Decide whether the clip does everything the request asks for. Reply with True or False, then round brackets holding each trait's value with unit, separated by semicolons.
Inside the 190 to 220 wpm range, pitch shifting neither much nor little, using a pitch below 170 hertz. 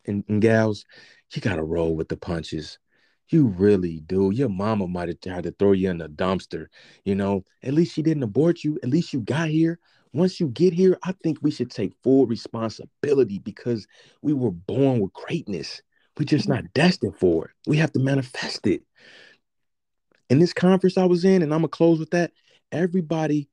False (195 wpm; 8.4 semitones; 135 Hz)